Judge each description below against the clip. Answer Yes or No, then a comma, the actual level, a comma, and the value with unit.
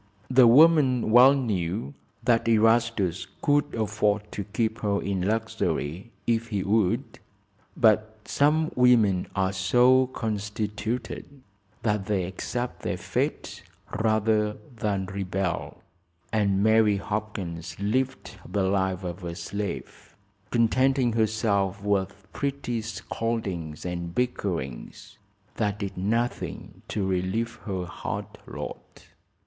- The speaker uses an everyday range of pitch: Yes, average, 3.3 semitones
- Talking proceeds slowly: Yes, slow, 110 wpm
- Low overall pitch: Yes, low, 105 Hz